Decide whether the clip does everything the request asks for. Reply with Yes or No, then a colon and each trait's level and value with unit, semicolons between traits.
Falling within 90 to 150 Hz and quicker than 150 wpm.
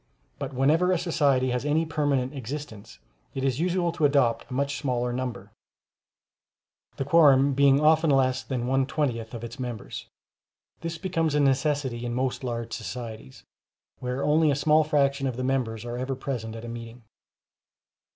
Yes: low, 135 Hz; average, 165 wpm